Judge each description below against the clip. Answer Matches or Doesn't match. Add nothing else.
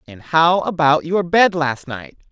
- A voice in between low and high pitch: Matches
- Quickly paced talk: Doesn't match